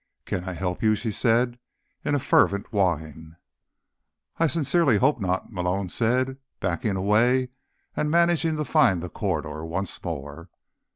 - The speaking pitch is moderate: No, low, 105 Hz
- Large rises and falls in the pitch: Yes, wide, 6.6 semitones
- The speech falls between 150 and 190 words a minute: No, average, 140 wpm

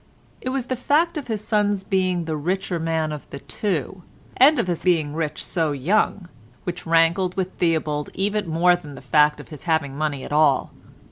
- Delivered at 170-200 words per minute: Yes, average, 195 wpm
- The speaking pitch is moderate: Yes, medium, 170 Hz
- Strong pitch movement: No, average, 4.1 semitones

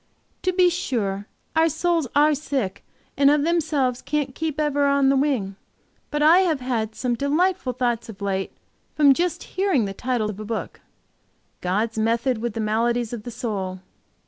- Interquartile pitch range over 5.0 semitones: Yes, wide, 5.4 semitones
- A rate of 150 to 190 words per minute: Yes, average, 170 wpm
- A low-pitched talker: No, very high, 260 Hz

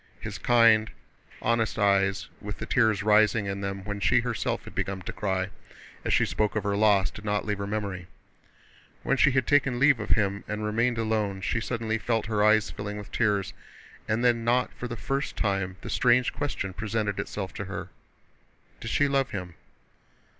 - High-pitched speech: No, low, 105 Hz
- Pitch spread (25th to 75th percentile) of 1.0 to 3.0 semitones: Yes, average, 2.7 semitones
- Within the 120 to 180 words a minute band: No, average, 190 wpm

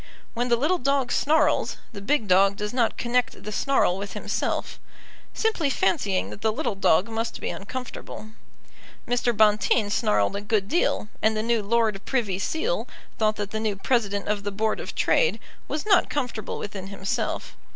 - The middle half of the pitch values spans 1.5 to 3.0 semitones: No, average, 3.9 semitones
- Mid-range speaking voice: No, high, 220 Hz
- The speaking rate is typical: Yes, average, 170 wpm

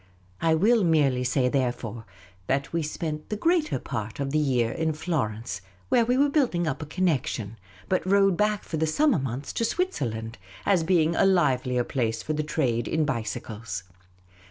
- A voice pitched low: No, medium, 150 Hz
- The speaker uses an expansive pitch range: Yes, wide, 7.0 semitones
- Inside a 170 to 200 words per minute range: Yes, average, 175 wpm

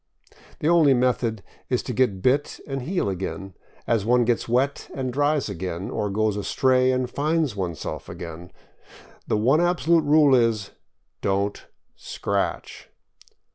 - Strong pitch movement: Yes, wide, 5.7 semitones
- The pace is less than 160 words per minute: Yes, slow, 135 wpm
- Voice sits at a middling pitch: No, low, 125 Hz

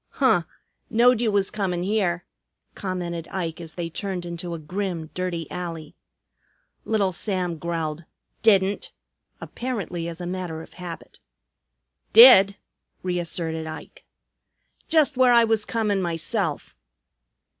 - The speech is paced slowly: Yes, slow, 120 wpm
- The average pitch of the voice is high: No, medium, 180 Hz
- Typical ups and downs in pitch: Yes, average, 3.6 semitones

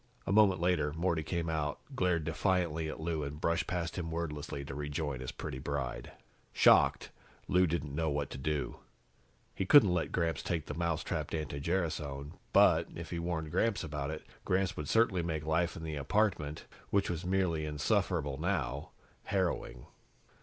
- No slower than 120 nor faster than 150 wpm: No, average, 165 wpm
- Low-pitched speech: Yes, very low, 80 Hz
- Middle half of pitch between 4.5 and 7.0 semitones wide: No, average, 3.2 semitones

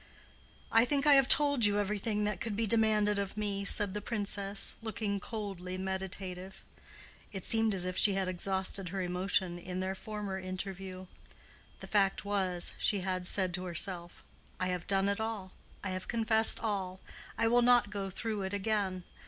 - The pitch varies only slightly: Yes, narrow, 2.3 semitones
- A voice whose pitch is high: Yes, high, 195 Hz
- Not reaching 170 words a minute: No, average, 175 wpm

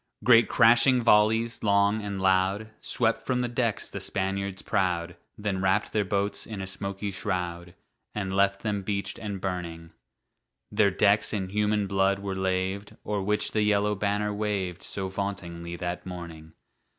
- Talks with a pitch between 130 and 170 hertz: No, low, 100 Hz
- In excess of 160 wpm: No, average, 155 wpm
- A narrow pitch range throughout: Yes, narrow, 1.9 semitones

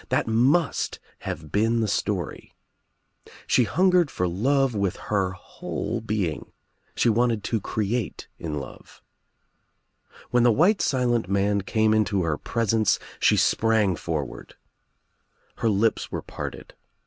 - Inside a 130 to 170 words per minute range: Yes, slow, 135 wpm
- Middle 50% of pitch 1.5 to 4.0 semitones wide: Yes, average, 3.6 semitones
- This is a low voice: Yes, low, 110 Hz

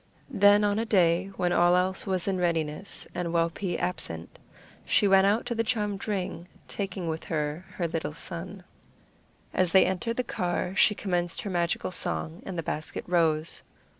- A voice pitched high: No, medium, 180 Hz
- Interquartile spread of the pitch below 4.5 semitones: Yes, average, 2.8 semitones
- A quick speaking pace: No, average, 170 wpm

